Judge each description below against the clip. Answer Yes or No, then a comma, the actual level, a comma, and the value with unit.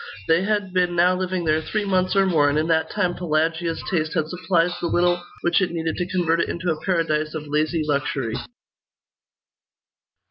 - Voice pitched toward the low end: No, medium, 170 Hz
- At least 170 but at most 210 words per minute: Yes, average, 185 wpm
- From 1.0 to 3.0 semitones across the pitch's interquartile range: Yes, narrow, 2.6 semitones